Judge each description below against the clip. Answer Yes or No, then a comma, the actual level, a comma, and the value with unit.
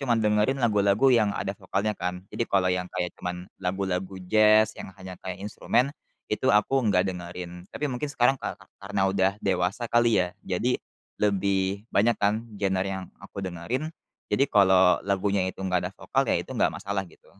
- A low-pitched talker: Yes, low, 100 Hz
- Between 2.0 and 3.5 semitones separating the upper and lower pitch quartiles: Yes, average, 2.8 semitones